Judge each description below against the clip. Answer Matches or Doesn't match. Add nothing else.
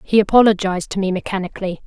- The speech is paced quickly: Doesn't match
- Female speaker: Matches